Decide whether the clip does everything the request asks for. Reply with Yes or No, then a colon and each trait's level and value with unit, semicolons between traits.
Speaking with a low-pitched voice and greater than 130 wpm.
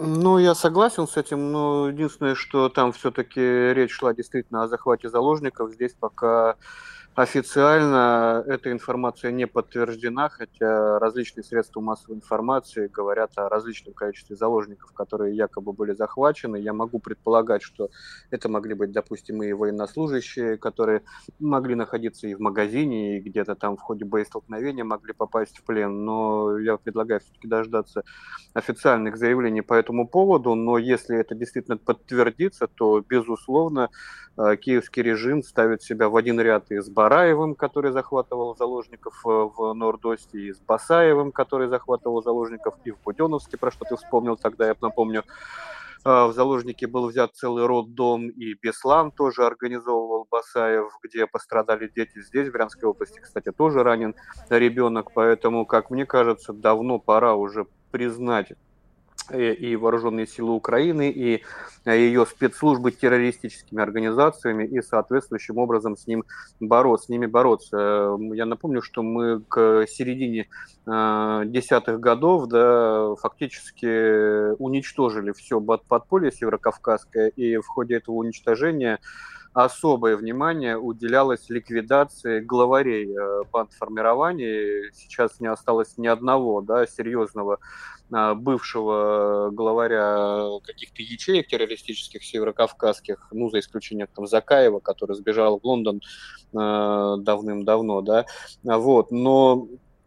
No: low, 115 Hz; average, 125 wpm